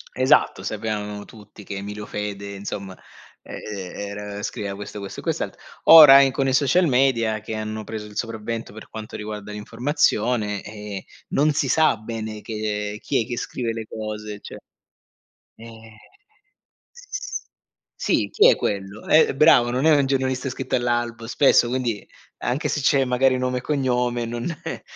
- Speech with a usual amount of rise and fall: Yes, average, 3.8 semitones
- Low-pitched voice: Yes, low, 115 Hz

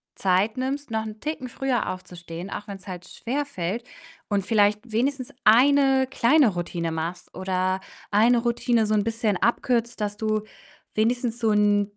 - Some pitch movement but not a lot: Yes, average, 4.0 semitones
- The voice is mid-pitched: No, high, 215 Hz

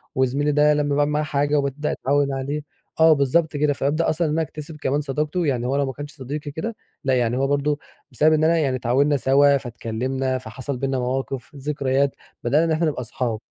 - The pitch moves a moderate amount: No, narrow, 2.3 semitones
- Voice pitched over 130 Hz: Yes, medium, 140 Hz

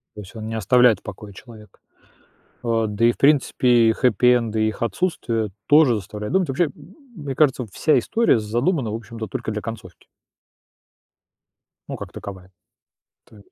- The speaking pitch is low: Yes, low, 115 Hz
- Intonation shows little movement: No, average, 3.3 semitones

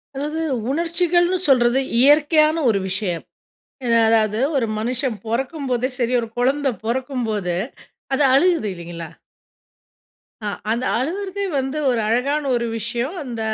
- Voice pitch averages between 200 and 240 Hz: No, very high, 255 Hz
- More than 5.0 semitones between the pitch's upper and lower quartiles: No, average, 4.6 semitones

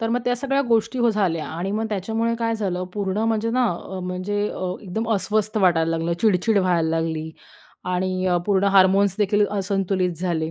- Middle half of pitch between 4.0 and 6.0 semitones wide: No, average, 3.3 semitones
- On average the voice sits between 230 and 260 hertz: No, high, 195 Hz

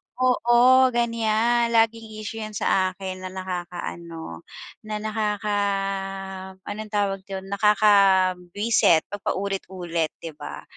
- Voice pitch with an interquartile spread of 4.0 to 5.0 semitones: No, average, 3.0 semitones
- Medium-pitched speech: No, high, 205 Hz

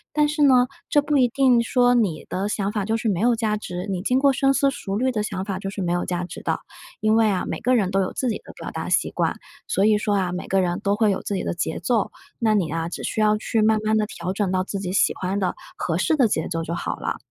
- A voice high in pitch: Yes, high, 210 Hz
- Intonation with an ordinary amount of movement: Yes, average, 4.3 semitones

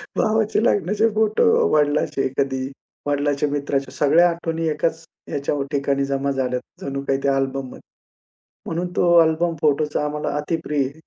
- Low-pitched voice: No, medium, 150 Hz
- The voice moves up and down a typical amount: Yes, average, 3.1 semitones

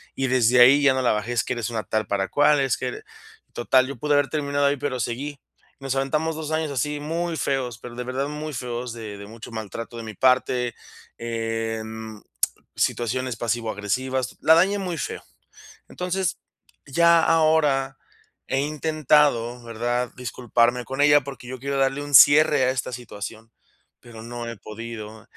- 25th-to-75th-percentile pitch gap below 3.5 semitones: No, average, 3.8 semitones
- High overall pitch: No, low, 130 Hz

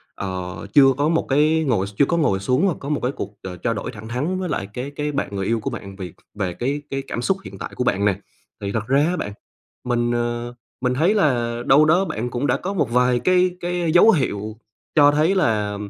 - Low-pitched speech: Yes, low, 125 Hz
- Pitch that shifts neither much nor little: No, wide, 6.1 semitones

